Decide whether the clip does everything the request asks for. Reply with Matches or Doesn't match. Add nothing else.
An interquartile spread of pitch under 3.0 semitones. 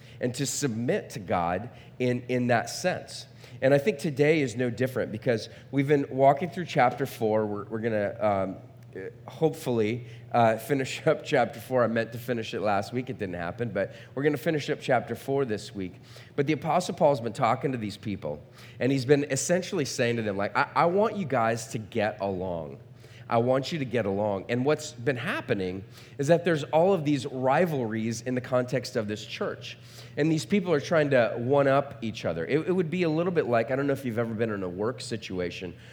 Doesn't match